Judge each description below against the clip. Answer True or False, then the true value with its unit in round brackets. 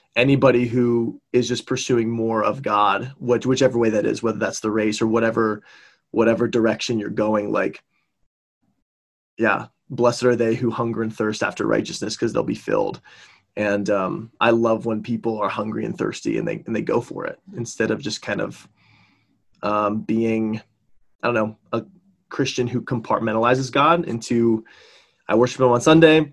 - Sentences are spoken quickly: False (175 wpm)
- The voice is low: True (115 Hz)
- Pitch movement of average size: False (2.2 semitones)